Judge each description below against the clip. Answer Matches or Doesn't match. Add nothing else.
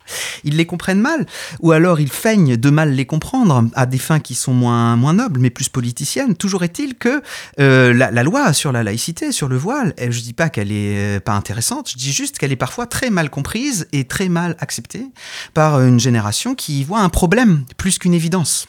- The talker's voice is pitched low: Doesn't match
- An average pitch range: Doesn't match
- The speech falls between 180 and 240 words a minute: Matches